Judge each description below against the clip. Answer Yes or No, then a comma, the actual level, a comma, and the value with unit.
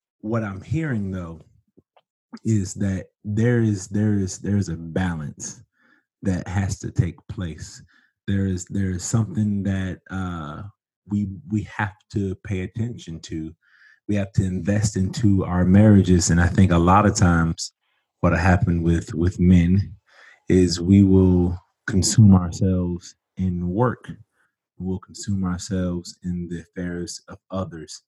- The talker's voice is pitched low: Yes, very low, 95 Hz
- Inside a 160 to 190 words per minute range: No, average, 145 wpm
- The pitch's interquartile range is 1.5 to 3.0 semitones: Yes, narrow, 2.5 semitones